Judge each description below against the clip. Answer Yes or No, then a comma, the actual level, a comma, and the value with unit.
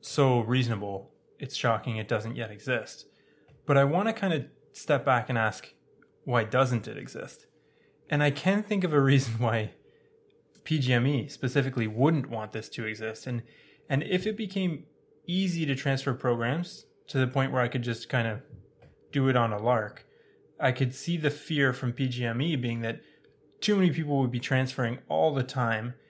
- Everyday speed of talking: Yes, average, 195 wpm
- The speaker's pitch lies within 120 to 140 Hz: Yes, low, 135 Hz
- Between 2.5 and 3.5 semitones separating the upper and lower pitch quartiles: No, average, 4.0 semitones